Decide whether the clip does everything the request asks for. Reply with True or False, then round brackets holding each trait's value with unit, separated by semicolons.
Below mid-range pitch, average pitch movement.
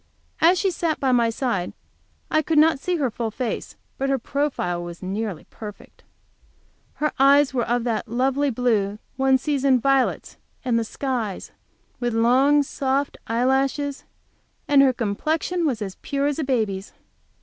False (260 Hz; 3.8 semitones)